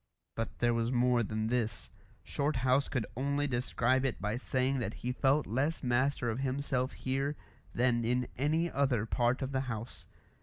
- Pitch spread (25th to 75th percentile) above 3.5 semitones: No, narrow, 2.4 semitones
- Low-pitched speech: Yes, low, 125 Hz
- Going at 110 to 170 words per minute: Yes, average, 165 wpm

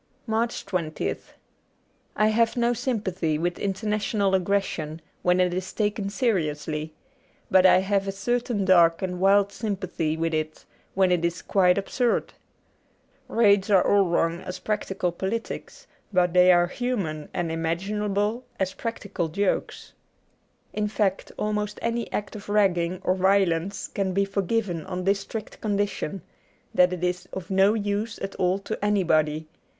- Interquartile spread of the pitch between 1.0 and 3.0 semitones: Yes, average, 2.7 semitones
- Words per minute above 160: No, average, 150 wpm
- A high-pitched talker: Yes, high, 195 Hz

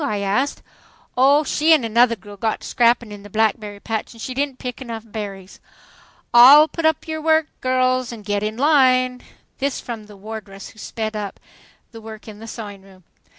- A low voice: No, high, 230 Hz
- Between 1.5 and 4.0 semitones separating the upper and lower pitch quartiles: Yes, average, 3.6 semitones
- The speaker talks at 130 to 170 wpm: No, average, 195 wpm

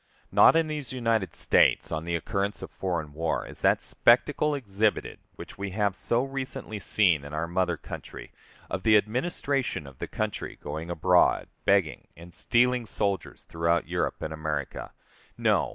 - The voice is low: Yes, very low, 95 Hz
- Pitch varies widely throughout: Yes, wide, 6.0 semitones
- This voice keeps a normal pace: Yes, average, 160 wpm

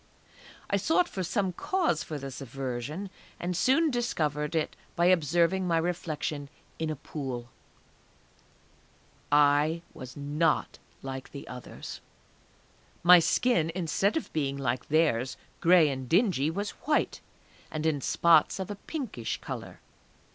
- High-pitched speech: No, medium, 160 Hz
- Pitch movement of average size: Yes, average, 4.5 semitones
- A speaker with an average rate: No, slow, 130 wpm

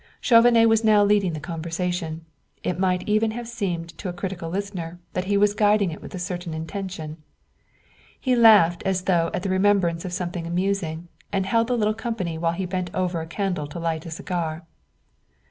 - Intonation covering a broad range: No, average, 3.4 semitones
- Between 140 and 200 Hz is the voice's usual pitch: Yes, medium, 185 Hz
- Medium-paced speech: Yes, average, 190 wpm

